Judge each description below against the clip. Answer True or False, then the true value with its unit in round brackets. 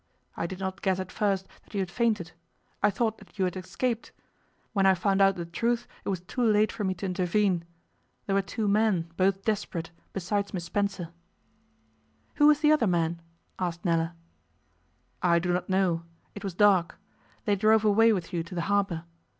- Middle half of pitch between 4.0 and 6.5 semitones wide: False (3.1 semitones)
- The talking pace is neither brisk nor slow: True (190 wpm)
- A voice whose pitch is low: False (195 Hz)